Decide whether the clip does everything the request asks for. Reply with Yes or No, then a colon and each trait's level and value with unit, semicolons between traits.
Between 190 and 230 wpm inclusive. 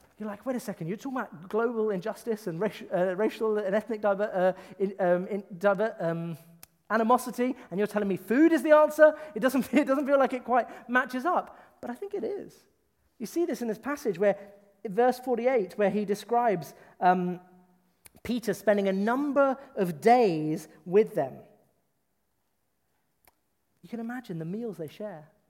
No: average, 180 wpm